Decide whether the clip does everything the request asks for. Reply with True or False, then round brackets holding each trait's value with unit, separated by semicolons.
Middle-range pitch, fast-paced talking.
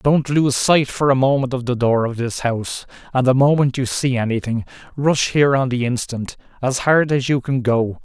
False (130 Hz; 215 wpm)